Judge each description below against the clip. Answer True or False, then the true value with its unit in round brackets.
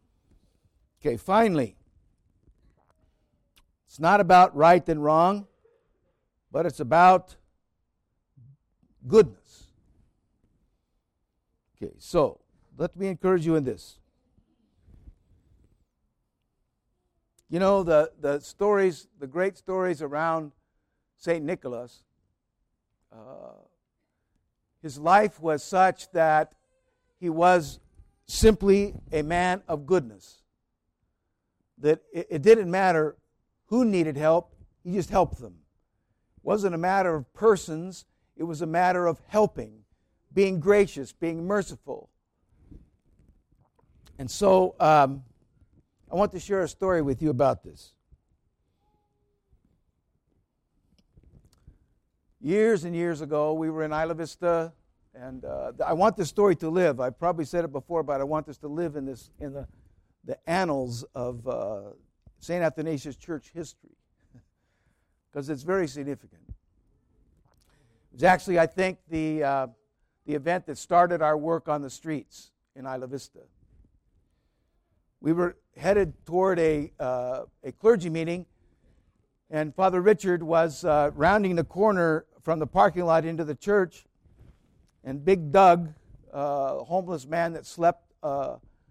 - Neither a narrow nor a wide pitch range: False (6.3 semitones)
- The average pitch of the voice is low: False (155 Hz)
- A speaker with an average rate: False (120 wpm)